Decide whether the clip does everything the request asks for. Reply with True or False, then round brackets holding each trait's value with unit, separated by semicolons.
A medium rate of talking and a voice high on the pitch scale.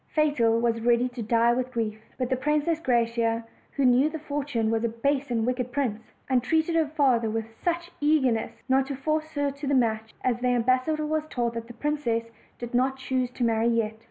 False (210 wpm; 250 Hz)